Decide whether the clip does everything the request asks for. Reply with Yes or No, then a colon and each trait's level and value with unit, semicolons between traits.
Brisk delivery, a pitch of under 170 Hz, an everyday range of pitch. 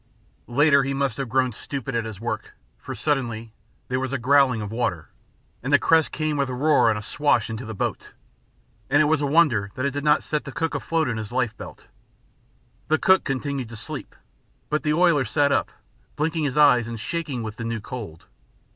Yes: fast, 210 wpm; low, 135 Hz; average, 4.4 semitones